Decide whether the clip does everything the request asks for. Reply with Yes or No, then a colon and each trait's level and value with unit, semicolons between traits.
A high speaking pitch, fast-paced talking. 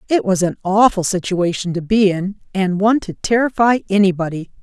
No: high, 195 Hz; average, 170 wpm